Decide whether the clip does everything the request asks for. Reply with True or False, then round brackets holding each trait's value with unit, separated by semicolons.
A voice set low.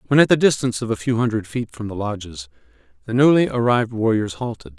True (110 Hz)